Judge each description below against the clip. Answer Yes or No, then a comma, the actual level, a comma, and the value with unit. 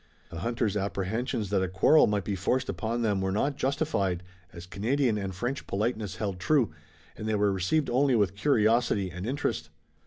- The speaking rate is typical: Yes, average, 180 wpm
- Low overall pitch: Yes, low, 105 Hz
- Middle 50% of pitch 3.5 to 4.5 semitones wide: Yes, average, 4.1 semitones